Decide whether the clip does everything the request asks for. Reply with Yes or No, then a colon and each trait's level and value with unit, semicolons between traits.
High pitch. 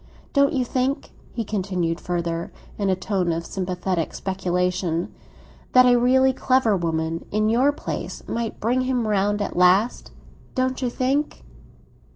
Yes: high, 205 Hz